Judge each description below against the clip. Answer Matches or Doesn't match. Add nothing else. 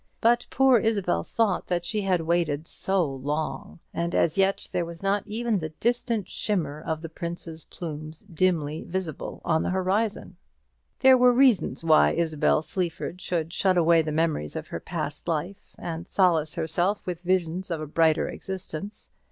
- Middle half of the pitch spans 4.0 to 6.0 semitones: Doesn't match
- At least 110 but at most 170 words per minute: Matches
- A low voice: Doesn't match